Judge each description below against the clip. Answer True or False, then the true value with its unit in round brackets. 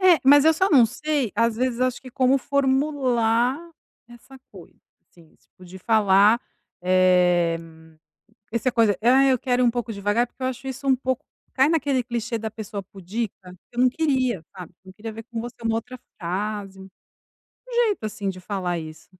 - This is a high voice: True (235 Hz)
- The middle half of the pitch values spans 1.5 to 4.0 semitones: False (4.6 semitones)